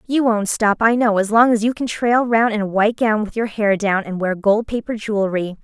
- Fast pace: Yes, fast, 265 wpm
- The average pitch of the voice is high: Yes, high, 215 Hz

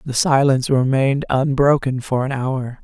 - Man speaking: No, female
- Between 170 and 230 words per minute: No, average, 150 wpm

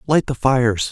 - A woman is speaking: No, male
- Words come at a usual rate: Yes, average, 195 wpm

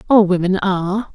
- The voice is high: Yes, high, 195 Hz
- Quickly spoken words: No, average, 155 wpm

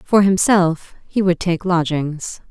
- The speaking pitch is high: No, medium, 175 Hz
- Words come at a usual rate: Yes, average, 145 wpm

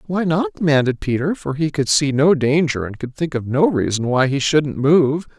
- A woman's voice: No, male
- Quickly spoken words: Yes, fast, 225 wpm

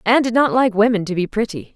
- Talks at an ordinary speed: No, fast, 275 wpm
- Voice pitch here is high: Yes, high, 220 Hz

